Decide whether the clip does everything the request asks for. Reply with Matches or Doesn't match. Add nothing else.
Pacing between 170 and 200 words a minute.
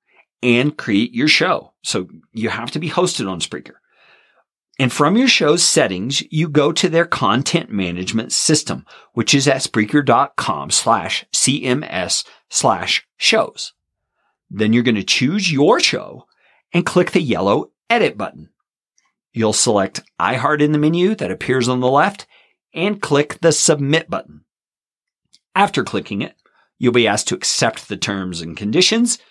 Doesn't match